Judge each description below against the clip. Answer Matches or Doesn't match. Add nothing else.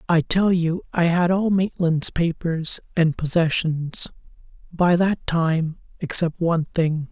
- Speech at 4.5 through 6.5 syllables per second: Doesn't match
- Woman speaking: Doesn't match